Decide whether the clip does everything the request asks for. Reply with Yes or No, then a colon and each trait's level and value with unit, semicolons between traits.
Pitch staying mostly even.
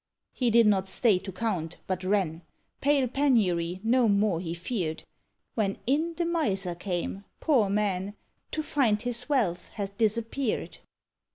No: average, 4.9 semitones